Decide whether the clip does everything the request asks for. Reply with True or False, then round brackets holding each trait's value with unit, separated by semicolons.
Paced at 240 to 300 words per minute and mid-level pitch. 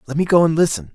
False (315 wpm; 150 Hz)